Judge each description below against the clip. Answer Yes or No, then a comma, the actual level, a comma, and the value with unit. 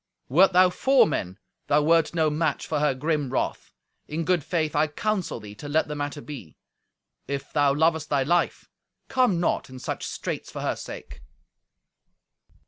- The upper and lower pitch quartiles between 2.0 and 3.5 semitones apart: Yes, average, 2.8 semitones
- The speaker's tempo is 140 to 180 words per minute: Yes, average, 170 wpm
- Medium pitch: Yes, medium, 150 Hz